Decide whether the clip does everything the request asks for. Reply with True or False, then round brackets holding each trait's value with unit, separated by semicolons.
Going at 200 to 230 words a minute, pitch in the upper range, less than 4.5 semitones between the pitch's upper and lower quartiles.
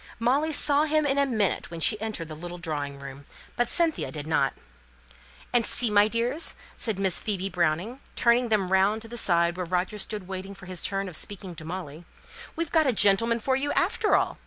False (205 wpm; 200 Hz; 5.4 semitones)